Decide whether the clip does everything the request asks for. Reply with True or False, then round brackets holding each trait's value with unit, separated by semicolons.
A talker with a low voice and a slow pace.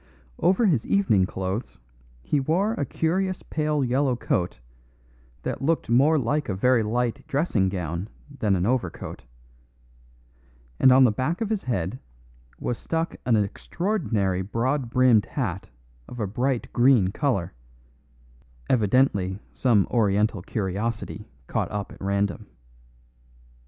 True (120 Hz; 125 wpm)